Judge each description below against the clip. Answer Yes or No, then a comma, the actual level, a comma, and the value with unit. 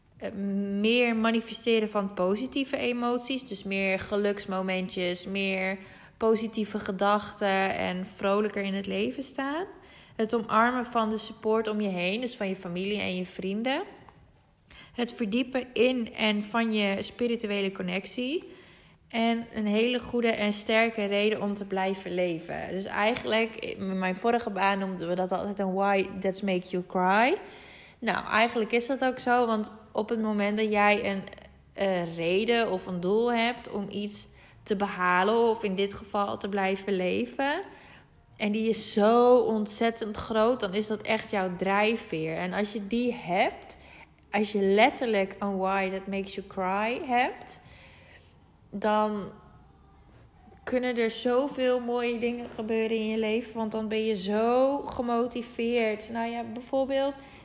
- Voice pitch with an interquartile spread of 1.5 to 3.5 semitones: Yes, average, 3.0 semitones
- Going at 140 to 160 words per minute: Yes, average, 150 wpm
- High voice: Yes, high, 215 Hz